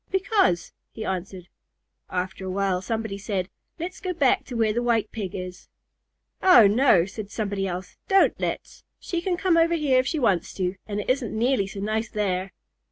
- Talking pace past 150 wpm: Yes, average, 185 wpm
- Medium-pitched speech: No, high, 215 Hz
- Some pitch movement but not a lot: No, wide, 5.8 semitones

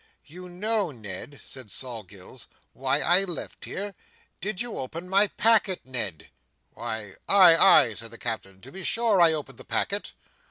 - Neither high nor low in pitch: Yes, medium, 165 Hz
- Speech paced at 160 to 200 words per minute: Yes, average, 165 wpm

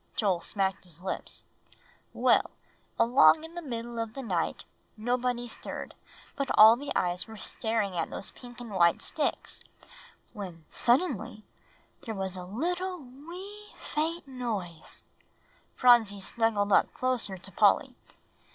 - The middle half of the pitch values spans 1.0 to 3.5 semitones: No, wide, 5.6 semitones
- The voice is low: No, high, 230 Hz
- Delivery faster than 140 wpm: No, slow, 135 wpm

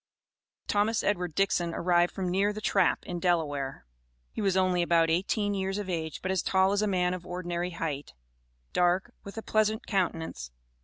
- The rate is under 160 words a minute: No, average, 175 wpm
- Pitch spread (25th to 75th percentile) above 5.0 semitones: No, narrow, 2.6 semitones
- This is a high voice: No, medium, 180 Hz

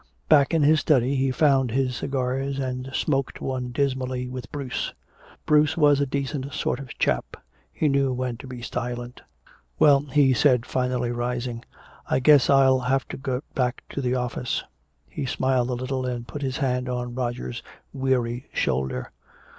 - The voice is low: Yes, low, 130 Hz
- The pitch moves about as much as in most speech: No, narrow, 1.8 semitones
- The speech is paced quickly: No, average, 165 wpm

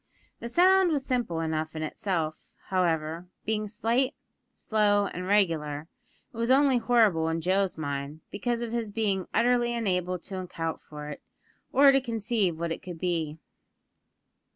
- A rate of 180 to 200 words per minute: No, average, 155 wpm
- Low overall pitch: No, high, 195 Hz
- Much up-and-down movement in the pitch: Yes, wide, 6.3 semitones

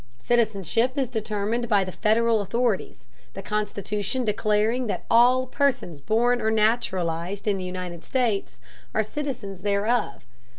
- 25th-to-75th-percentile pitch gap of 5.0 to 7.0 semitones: No, average, 3.3 semitones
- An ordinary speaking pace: No, slow, 130 wpm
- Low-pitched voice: No, high, 215 Hz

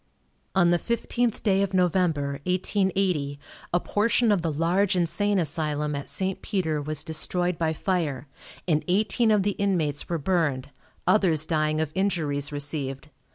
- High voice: No, medium, 170 Hz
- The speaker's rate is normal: Yes, average, 150 wpm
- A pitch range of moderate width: Yes, average, 4.2 semitones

